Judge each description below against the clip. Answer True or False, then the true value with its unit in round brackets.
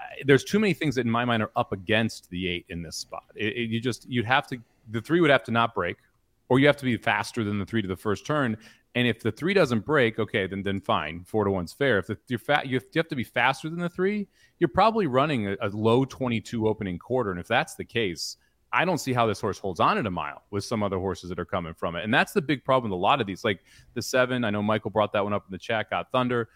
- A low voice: True (115 Hz)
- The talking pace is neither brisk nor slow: False (290 wpm)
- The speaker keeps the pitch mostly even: False (4.2 semitones)